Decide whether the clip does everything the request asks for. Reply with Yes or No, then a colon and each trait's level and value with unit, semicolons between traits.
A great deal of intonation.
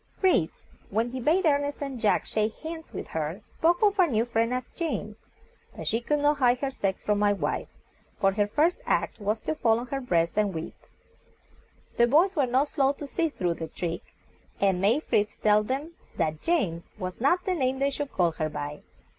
Yes: wide, 6.4 semitones